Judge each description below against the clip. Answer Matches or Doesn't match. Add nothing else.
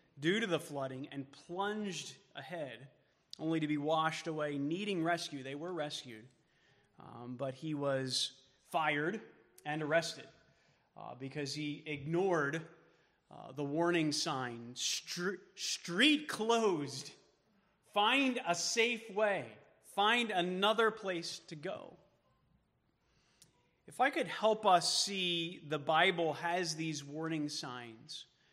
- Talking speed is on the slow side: Matches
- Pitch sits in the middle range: Matches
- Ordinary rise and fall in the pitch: Matches